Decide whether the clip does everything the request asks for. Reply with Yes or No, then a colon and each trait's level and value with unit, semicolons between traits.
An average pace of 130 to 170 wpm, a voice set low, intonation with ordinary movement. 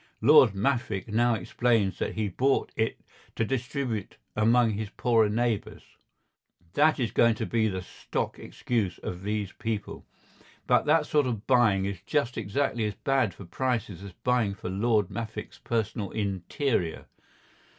Yes: average, 140 wpm; low, 110 Hz; average, 3.4 semitones